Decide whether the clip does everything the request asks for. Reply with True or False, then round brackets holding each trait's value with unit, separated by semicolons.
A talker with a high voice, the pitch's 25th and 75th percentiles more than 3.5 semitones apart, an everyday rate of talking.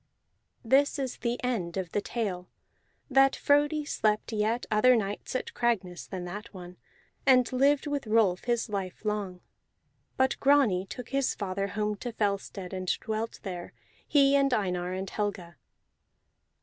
True (215 Hz; 5.1 semitones; 150 wpm)